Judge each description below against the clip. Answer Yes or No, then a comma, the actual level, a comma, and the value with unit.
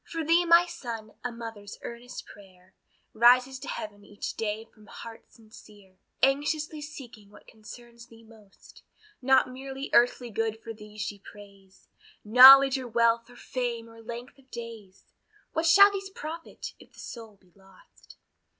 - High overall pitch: Yes, high, 235 Hz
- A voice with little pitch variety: No, average, 4.0 semitones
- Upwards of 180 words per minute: No, average, 155 wpm